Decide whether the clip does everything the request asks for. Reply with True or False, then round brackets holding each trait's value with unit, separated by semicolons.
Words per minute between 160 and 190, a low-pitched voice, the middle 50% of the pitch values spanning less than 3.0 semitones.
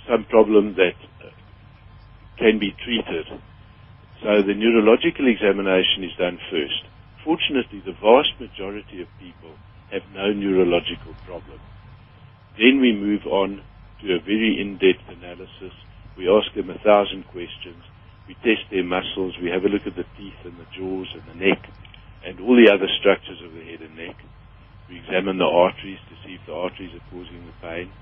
True (170 wpm; 100 Hz; 2.4 semitones)